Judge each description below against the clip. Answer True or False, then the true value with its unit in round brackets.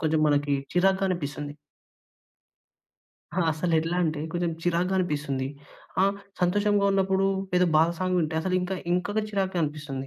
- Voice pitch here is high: False (175 Hz)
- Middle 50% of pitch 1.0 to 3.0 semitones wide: False (3.7 semitones)